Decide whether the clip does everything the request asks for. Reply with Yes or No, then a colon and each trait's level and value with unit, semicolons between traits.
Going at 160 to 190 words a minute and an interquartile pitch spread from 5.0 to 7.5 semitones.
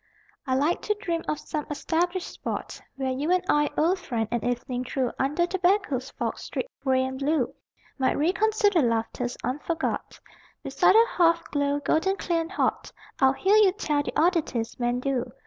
Yes: average, 170 wpm; wide, 5.4 semitones